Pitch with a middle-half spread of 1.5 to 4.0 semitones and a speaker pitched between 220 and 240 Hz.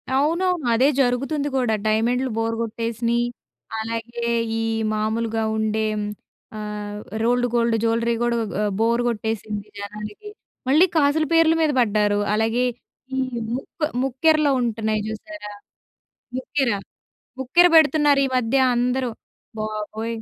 Yes: average, 3.7 semitones; high, 235 Hz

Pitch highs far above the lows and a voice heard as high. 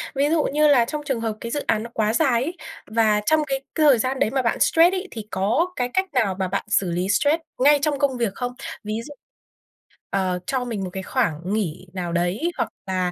Yes: wide, 6.6 semitones; high, 235 Hz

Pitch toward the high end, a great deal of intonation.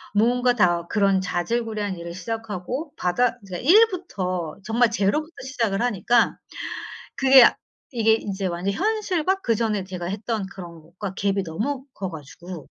No: high, 210 Hz; average, 5.0 semitones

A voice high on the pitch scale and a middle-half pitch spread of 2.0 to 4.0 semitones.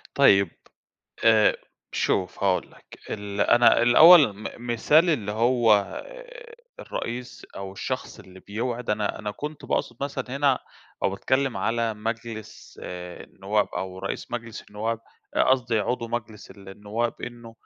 No: low, 115 Hz; average, 3.0 semitones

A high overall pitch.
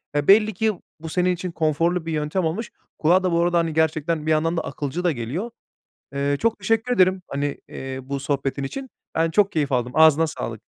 No: medium, 165 Hz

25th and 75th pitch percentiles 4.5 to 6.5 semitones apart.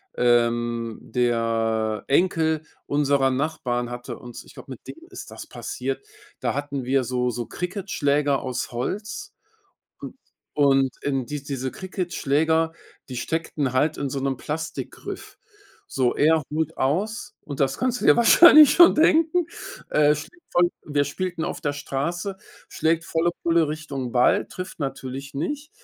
Yes: average, 4.8 semitones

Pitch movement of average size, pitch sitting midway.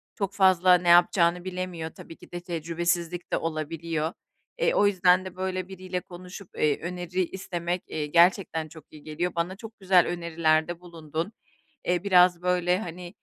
No: narrow, 1.7 semitones; medium, 175 Hz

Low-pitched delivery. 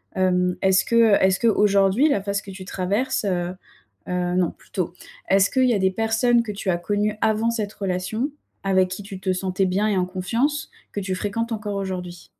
No: high, 195 Hz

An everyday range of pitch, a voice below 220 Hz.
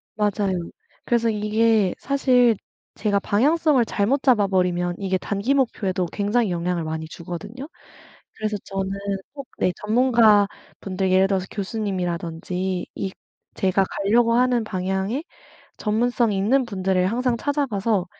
Yes: average, 4.0 semitones; high, 205 Hz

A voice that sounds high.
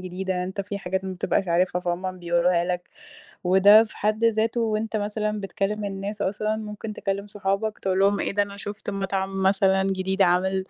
Yes: high, 195 Hz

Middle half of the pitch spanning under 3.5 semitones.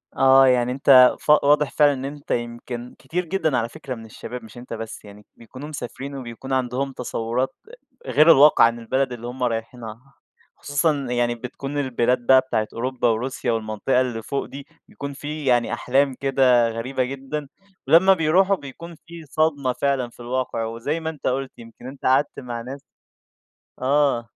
Yes: average, 2.9 semitones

